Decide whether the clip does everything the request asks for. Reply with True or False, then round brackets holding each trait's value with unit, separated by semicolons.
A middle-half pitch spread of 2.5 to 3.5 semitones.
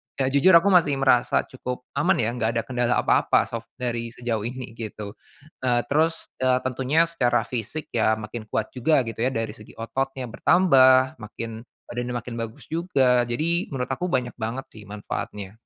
True (2.8 semitones)